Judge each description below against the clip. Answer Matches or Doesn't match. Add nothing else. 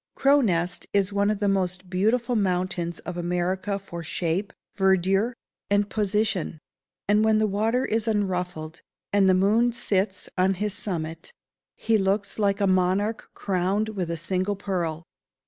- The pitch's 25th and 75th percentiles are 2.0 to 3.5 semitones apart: Matches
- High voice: Matches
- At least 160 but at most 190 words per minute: Doesn't match